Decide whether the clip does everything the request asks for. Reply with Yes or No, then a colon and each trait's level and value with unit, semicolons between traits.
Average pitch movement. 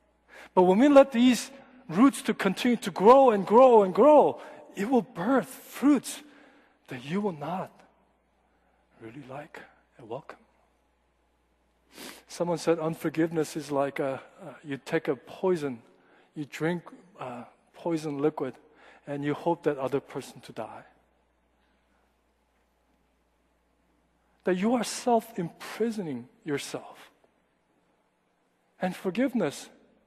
No: wide, 8.9 semitones